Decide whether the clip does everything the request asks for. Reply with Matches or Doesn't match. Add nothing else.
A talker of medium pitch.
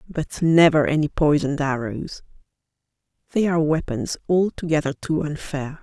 Matches